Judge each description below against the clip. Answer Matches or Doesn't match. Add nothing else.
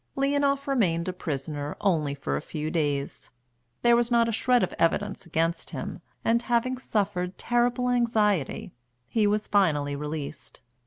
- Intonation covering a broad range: Matches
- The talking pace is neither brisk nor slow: Matches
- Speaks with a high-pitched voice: Matches